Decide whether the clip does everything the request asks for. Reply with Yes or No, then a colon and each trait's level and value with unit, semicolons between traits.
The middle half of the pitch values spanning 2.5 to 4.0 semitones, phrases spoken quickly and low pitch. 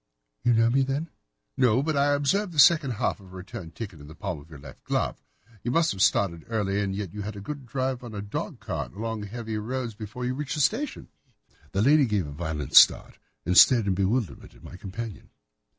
No: average, 5.3 semitones; fast, 225 wpm; low, 110 Hz